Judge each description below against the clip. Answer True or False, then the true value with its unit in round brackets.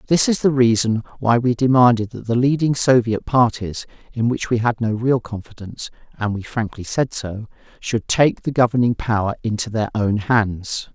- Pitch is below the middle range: True (115 Hz)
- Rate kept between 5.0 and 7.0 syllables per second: False (4.6 syllables/s)